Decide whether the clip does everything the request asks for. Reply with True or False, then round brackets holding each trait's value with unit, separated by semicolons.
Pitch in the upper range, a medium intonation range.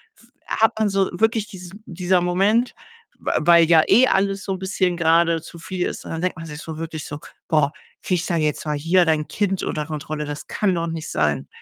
False (170 Hz; 3.4 semitones)